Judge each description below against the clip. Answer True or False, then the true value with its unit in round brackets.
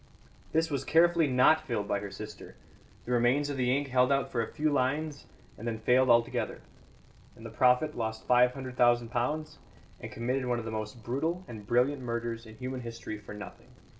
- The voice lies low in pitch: True (125 Hz)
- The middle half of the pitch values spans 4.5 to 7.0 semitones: False (3.1 semitones)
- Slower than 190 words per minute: False (195 wpm)